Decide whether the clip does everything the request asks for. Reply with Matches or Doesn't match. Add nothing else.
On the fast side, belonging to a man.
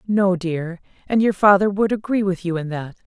Doesn't match